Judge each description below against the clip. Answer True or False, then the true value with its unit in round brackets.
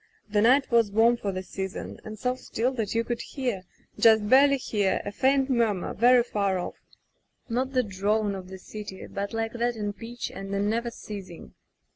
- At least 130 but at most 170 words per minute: False (200 wpm)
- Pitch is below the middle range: False (220 Hz)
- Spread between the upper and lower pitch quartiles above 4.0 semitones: False (3.3 semitones)